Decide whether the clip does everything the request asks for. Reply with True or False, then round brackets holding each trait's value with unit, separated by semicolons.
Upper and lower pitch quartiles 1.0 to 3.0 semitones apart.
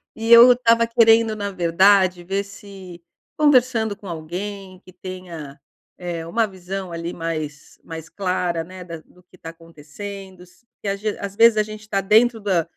False (3.8 semitones)